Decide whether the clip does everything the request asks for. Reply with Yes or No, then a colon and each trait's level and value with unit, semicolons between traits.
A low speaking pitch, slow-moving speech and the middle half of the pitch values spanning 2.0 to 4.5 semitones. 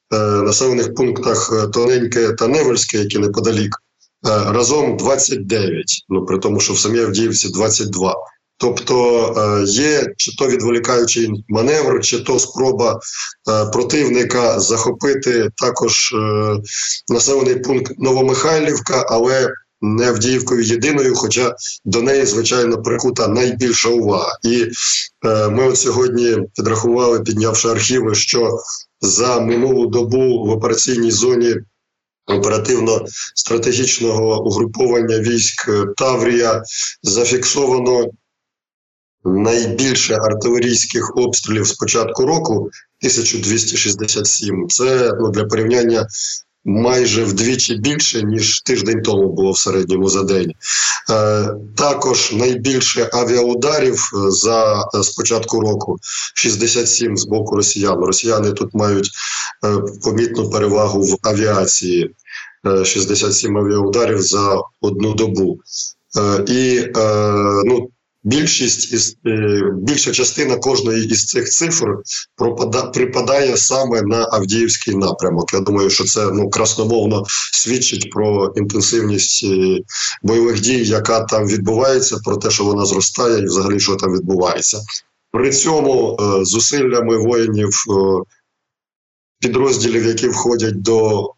Yes: low, 110 Hz; slow, 100 wpm; average, 2.7 semitones